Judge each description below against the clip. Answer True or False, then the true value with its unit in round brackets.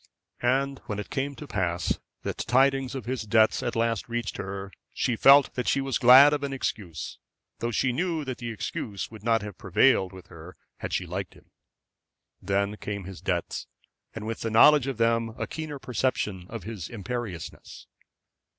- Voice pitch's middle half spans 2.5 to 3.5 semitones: False (5.0 semitones)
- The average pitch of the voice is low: True (115 Hz)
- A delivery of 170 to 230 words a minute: True (180 wpm)